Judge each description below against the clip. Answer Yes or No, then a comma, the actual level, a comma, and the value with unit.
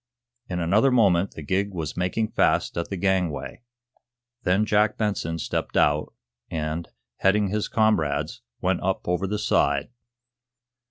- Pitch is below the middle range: Yes, very low, 95 Hz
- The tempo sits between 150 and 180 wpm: No, average, 140 wpm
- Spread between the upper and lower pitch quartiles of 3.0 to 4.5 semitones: Yes, average, 4.0 semitones